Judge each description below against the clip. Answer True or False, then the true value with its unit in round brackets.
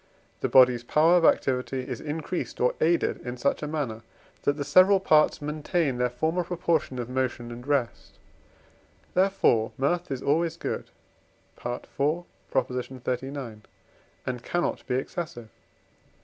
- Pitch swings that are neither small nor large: True (4.6 semitones)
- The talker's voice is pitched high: False (140 Hz)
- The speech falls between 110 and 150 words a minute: True (135 wpm)